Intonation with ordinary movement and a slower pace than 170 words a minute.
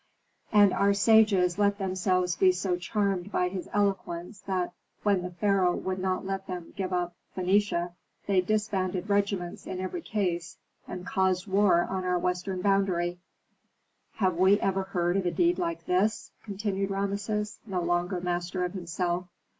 No: narrow, 2.0 semitones; average, 155 wpm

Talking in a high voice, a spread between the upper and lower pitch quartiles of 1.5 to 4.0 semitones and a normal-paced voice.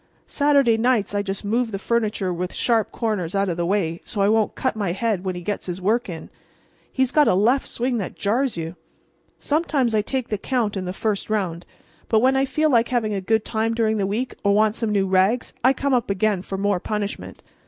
No: high, 215 Hz; average, 3.6 semitones; fast, 230 wpm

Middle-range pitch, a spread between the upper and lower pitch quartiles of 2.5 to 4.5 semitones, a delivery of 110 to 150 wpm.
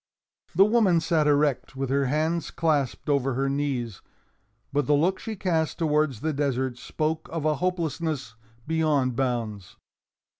Yes: medium, 150 Hz; average, 3.3 semitones; average, 145 wpm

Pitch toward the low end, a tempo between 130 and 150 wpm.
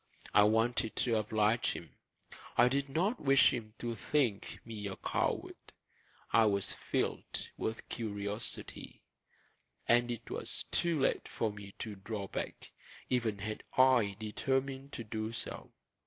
Yes: low, 115 Hz; average, 140 wpm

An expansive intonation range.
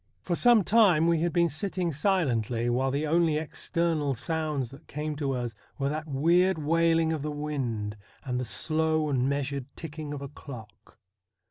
No: average, 3.3 semitones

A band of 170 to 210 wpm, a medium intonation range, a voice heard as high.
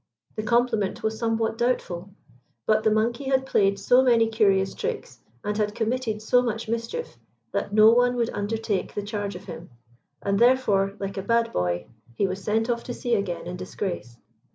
Yes: average, 180 wpm; average, 3.0 semitones; high, 220 Hz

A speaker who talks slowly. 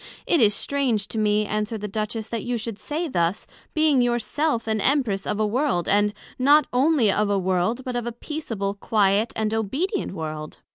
No: average, 195 wpm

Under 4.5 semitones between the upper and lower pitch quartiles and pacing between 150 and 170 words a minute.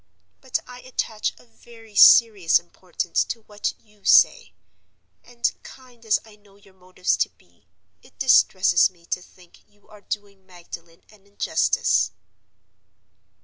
No: average, 3.7 semitones; average, 140 wpm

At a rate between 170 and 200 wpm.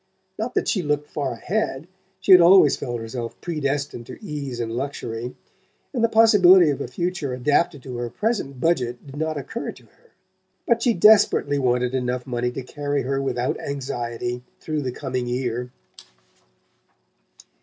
No: average, 160 wpm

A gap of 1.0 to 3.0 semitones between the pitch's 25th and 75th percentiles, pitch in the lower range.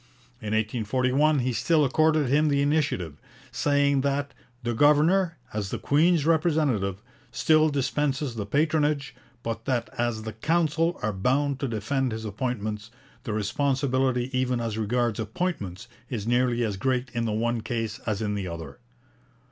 No: average, 4.8 semitones; low, 125 Hz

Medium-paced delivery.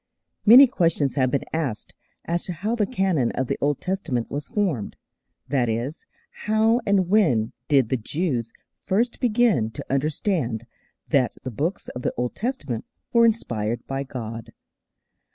Yes: average, 155 wpm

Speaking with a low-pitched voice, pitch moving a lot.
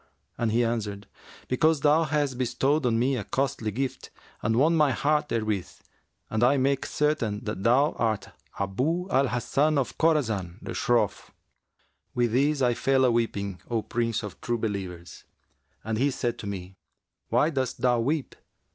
No: low, 120 Hz; average, 4.3 semitones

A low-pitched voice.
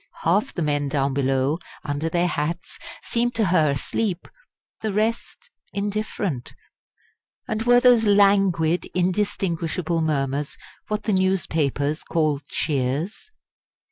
No: medium, 170 Hz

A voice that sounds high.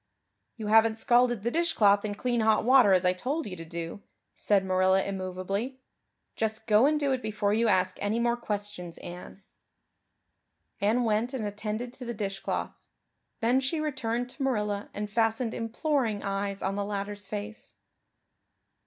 Yes: high, 215 Hz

